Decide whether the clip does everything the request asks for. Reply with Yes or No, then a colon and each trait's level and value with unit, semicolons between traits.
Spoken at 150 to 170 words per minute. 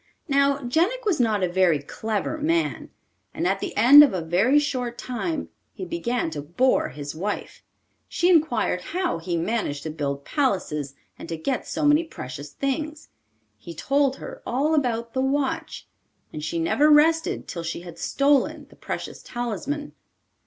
Yes: average, 165 wpm